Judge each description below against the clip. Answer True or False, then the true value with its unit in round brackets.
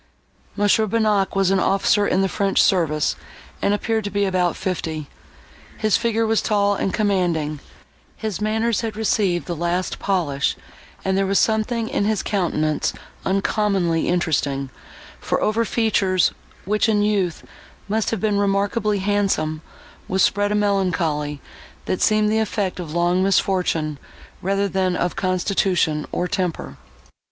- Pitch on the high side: True (195 Hz)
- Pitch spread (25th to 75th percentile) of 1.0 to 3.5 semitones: True (3.1 semitones)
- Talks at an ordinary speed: True (145 wpm)